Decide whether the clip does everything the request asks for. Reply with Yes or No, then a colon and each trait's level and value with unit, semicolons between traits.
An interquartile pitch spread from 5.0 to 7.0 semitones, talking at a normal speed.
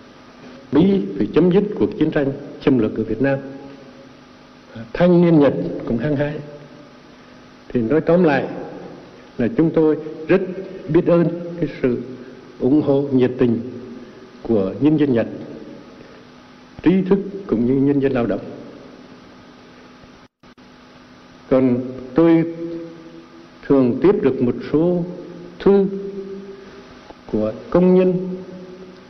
No: wide, 5.6 semitones; slow, 120 wpm